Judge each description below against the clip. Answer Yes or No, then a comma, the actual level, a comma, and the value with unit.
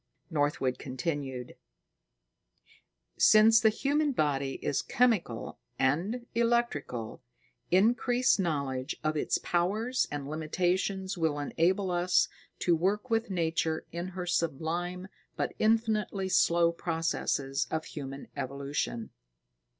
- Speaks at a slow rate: Yes, slow, 105 wpm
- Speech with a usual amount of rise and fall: No, wide, 6.2 semitones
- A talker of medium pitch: Yes, medium, 170 Hz